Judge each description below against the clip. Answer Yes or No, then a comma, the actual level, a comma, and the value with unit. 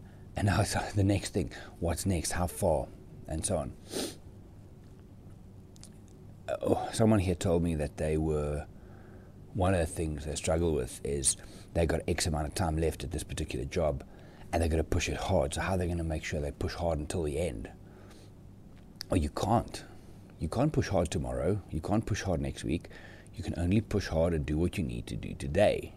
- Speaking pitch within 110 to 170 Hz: No, very low, 90 Hz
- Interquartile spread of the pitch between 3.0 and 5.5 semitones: Yes, average, 3.4 semitones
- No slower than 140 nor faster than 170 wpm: No, fast, 205 wpm